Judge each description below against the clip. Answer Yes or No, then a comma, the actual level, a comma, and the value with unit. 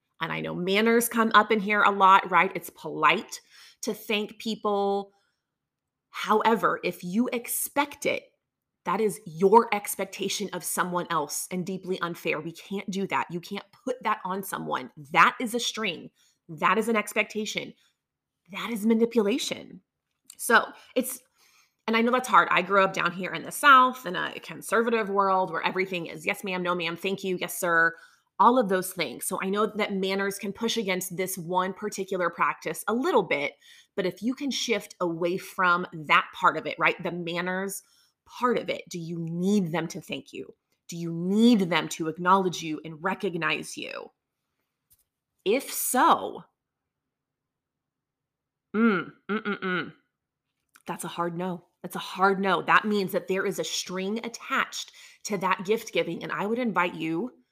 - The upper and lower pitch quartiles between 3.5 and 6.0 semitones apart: Yes, average, 3.8 semitones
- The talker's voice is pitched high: Yes, high, 195 Hz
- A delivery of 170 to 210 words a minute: Yes, average, 175 wpm